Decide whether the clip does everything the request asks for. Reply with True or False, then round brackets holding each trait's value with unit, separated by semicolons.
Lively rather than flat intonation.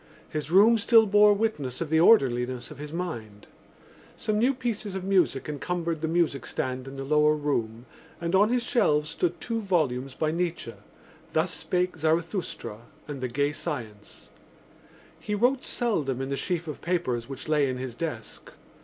True (5.9 semitones)